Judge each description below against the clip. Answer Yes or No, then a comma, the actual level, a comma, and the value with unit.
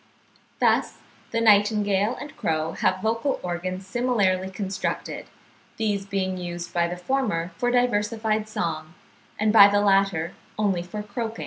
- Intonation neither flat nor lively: Yes, average, 3.3 semitones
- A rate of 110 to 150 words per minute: Yes, slow, 135 wpm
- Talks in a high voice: Yes, high, 200 Hz